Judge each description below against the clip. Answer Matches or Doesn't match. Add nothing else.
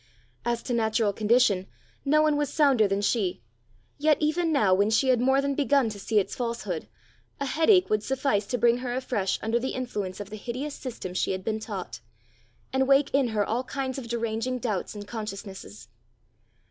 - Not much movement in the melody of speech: Doesn't match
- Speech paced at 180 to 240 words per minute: Matches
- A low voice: Doesn't match